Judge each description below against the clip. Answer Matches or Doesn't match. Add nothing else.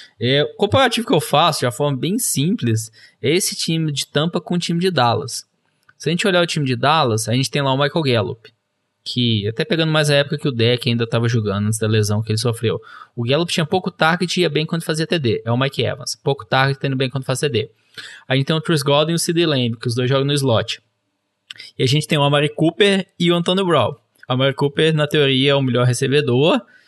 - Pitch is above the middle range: Doesn't match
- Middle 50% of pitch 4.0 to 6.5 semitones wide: Matches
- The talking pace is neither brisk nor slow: Doesn't match